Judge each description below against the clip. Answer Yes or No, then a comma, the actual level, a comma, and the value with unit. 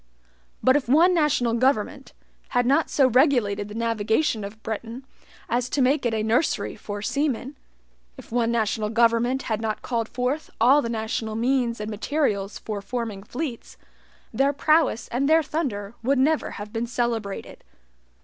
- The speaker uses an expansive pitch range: No, average, 3.7 semitones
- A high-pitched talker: Yes, high, 235 Hz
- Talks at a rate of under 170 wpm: Yes, average, 160 wpm